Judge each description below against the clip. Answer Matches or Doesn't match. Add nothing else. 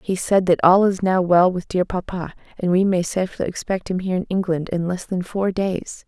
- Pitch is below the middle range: Doesn't match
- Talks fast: Matches